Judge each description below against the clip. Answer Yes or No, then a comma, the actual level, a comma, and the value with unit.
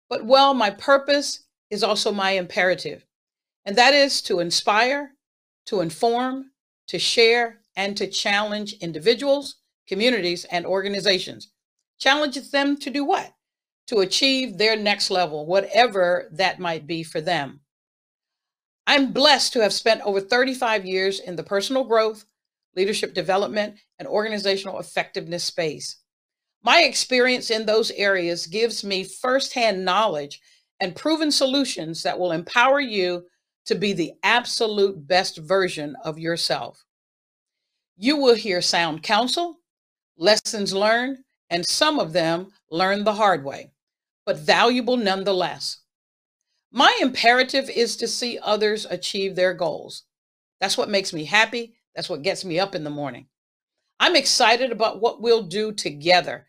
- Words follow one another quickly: No, slow, 135 wpm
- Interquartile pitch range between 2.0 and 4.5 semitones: No, average, 5.1 semitones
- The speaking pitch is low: No, high, 210 Hz